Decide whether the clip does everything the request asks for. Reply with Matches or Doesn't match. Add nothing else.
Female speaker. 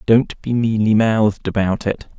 Doesn't match